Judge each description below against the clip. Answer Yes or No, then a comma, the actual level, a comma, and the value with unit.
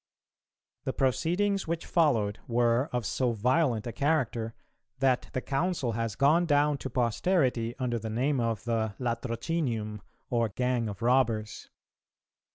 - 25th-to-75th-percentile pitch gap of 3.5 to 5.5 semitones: Yes, average, 3.9 semitones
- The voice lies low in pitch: Yes, low, 125 Hz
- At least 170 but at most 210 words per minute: No, slow, 135 wpm